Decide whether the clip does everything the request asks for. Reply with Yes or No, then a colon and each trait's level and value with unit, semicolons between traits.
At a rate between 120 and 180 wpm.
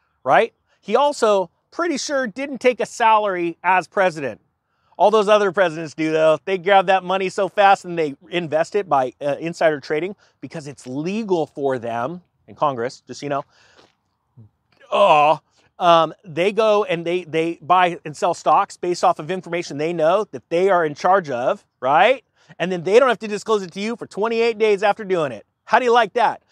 No: average, 195 wpm